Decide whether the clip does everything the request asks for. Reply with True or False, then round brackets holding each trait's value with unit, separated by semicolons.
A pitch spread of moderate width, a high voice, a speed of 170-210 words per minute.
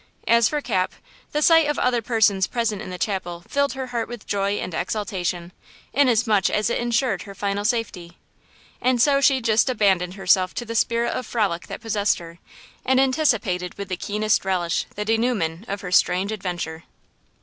True (4.5 semitones; 210 Hz; 180 wpm)